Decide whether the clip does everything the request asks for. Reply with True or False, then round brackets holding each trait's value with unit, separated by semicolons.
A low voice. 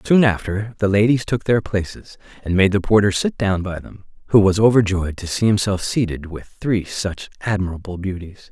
True (100 Hz)